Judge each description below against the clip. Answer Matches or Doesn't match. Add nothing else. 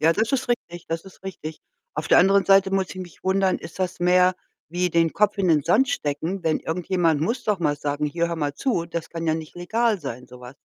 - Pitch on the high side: Doesn't match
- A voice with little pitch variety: Doesn't match